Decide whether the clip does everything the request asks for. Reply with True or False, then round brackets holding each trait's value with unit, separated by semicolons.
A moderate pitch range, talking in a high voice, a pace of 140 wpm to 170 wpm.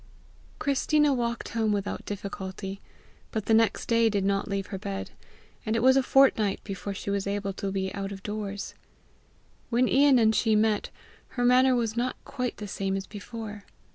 False (3.1 semitones; 215 Hz; 180 wpm)